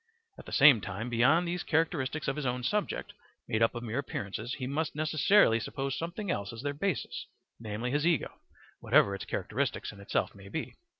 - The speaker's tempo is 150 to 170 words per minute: No, average, 190 wpm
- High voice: No, low, 135 Hz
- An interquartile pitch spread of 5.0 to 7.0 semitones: Yes, wide, 5.5 semitones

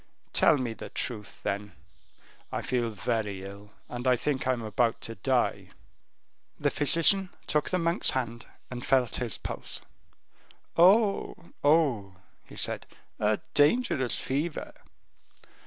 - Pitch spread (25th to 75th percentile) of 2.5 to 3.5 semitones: No, wide, 5.4 semitones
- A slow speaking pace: Yes, slow, 130 wpm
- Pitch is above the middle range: No, low, 125 Hz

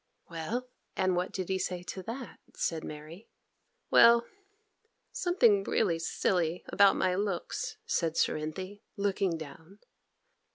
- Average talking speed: No, slow, 120 wpm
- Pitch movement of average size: Yes, average, 3.7 semitones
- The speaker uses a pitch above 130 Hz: Yes, medium, 185 Hz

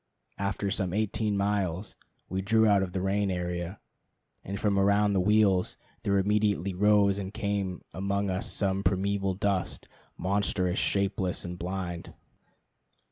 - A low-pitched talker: Yes, low, 100 Hz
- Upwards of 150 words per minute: No, slow, 135 wpm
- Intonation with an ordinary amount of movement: No, narrow, 1.6 semitones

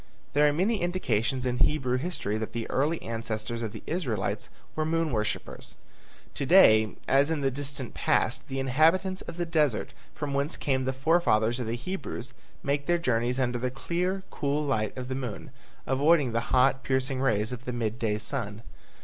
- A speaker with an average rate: Yes, average, 185 wpm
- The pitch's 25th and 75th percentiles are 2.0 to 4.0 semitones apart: No, average, 4.6 semitones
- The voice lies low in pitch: Yes, low, 130 Hz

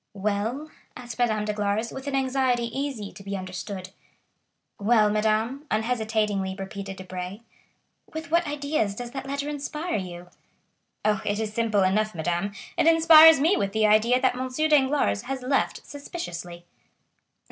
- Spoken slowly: No, average, 145 wpm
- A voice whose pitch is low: No, high, 220 Hz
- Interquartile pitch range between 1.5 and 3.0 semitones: No, average, 5.3 semitones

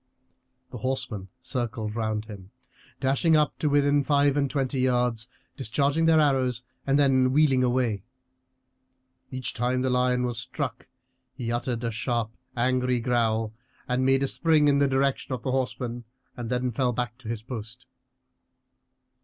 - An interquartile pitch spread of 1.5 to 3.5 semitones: Yes, narrow, 2.5 semitones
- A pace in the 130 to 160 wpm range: Yes, average, 155 wpm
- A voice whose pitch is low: Yes, low, 125 Hz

